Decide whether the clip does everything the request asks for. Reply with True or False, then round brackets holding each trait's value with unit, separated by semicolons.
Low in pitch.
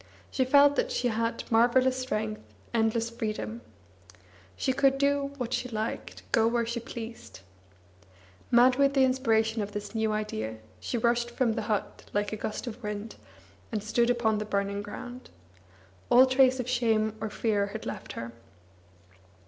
False (230 Hz)